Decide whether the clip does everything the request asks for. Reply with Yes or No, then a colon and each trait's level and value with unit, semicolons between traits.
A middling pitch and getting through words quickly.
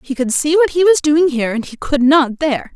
No: very high, 290 Hz; fast, 285 wpm